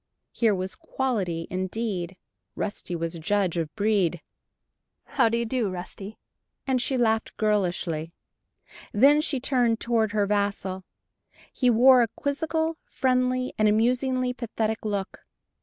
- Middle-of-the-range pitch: No, high, 220 Hz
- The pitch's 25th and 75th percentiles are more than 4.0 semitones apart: Yes, average, 5.0 semitones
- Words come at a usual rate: No, slow, 130 wpm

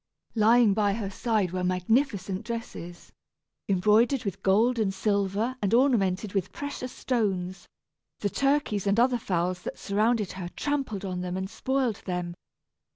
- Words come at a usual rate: Yes, average, 145 wpm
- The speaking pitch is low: No, high, 205 Hz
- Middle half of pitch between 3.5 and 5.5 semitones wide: Yes, average, 4.0 semitones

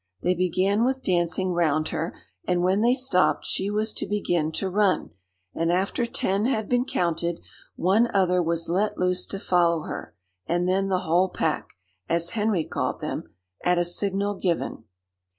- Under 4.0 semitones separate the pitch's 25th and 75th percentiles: Yes, average, 2.9 semitones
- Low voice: No, medium, 185 Hz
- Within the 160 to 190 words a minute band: Yes, average, 170 wpm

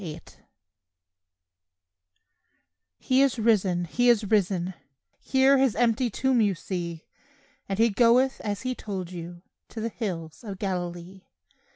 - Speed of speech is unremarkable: No, slow, 130 wpm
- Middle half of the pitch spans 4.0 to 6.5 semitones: Yes, average, 5.2 semitones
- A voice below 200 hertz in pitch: No, high, 205 Hz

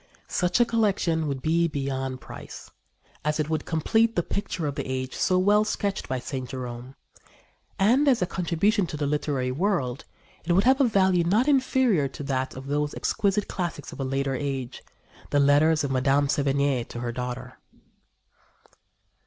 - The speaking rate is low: No, average, 170 wpm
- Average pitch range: No, wide, 6.2 semitones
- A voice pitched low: No, medium, 150 Hz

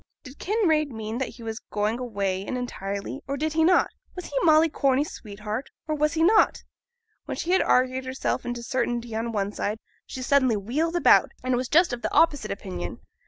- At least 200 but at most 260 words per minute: Yes, fast, 205 wpm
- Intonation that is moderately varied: No, wide, 5.7 semitones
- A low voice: No, very high, 255 Hz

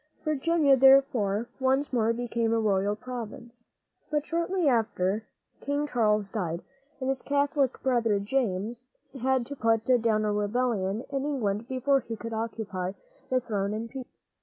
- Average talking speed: Yes, average, 145 wpm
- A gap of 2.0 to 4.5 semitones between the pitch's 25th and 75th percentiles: Yes, average, 4.0 semitones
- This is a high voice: Yes, high, 235 Hz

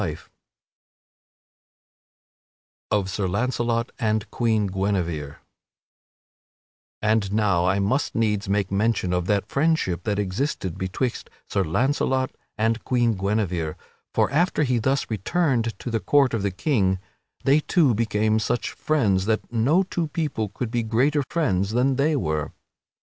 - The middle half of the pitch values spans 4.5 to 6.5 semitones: Yes, average, 4.9 semitones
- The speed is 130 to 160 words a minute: Yes, slow, 135 wpm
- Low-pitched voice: Yes, low, 110 Hz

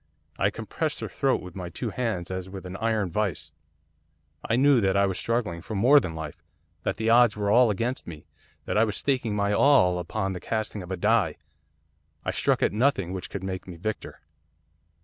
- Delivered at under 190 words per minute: No, fast, 205 wpm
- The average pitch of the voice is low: Yes, low, 100 Hz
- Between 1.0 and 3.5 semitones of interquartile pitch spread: No, average, 3.9 semitones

